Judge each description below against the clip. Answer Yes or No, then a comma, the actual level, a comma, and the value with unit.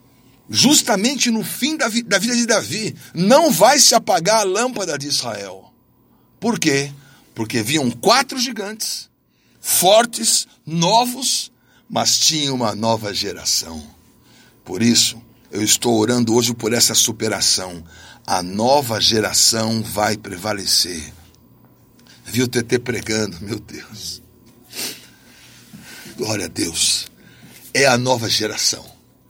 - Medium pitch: No, low, 125 Hz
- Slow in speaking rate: Yes, slow, 115 wpm